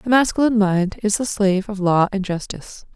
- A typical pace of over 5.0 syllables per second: Yes, 5.8 syllables/s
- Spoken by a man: No, female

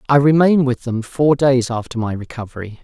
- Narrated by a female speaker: No, male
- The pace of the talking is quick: No, average, 190 wpm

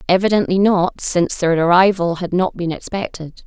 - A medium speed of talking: Yes, average, 155 wpm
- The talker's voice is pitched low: No, medium, 180 Hz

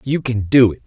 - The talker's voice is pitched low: Yes, low, 120 Hz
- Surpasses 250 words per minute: Yes, fast, 275 wpm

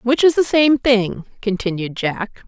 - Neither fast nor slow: Yes, average, 170 wpm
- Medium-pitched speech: No, high, 230 Hz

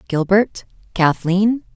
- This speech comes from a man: No, female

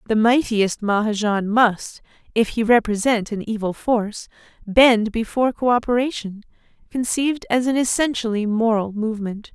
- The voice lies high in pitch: Yes, high, 225 Hz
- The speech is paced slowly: Yes, slow, 120 wpm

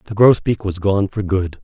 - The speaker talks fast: Yes, fast, 220 wpm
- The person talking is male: Yes, male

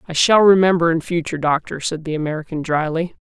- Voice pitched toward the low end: No, medium, 165 Hz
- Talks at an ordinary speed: Yes, average, 185 wpm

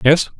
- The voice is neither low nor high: Yes, medium, 150 Hz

